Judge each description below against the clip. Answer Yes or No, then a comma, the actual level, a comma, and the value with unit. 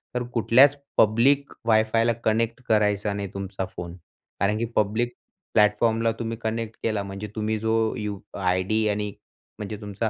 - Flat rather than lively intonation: Yes, narrow, 2.0 semitones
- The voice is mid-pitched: No, low, 110 Hz